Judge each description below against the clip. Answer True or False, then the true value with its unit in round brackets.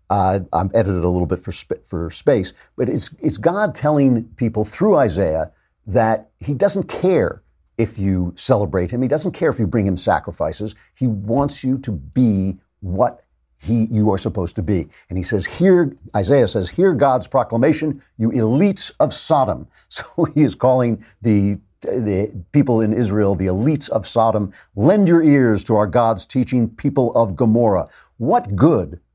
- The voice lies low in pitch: True (110 Hz)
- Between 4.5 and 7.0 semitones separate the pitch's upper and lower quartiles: True (5.3 semitones)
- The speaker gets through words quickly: False (175 wpm)